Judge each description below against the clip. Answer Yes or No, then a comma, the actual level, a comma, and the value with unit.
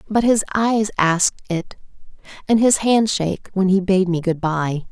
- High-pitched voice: Yes, high, 195 Hz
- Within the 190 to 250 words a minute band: No, average, 160 wpm